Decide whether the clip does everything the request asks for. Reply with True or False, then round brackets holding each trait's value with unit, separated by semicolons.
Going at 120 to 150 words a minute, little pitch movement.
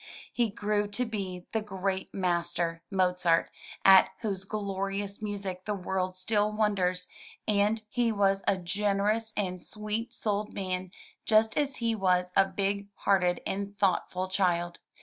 True (140 wpm; 2.3 semitones)